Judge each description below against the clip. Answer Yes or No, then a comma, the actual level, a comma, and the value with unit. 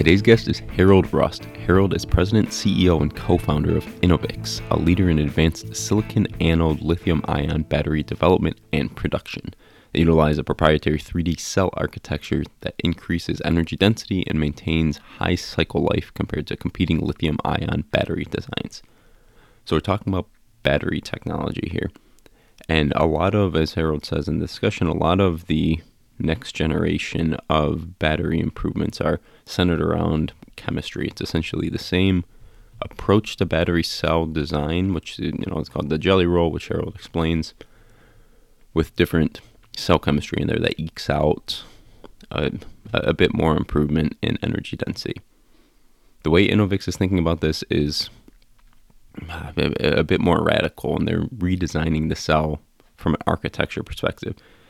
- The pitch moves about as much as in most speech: Yes, average, 3.6 semitones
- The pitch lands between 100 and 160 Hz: No, very low, 85 Hz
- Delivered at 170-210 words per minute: No, average, 150 wpm